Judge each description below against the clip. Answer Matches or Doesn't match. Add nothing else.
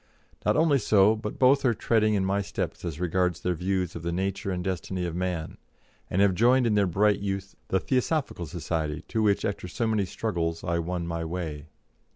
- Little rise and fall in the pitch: Doesn't match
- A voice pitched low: Matches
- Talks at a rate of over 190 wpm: Matches